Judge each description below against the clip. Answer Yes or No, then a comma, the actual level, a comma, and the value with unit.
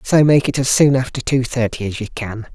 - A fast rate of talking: Yes, fast, 260 wpm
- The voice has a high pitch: No, low, 125 Hz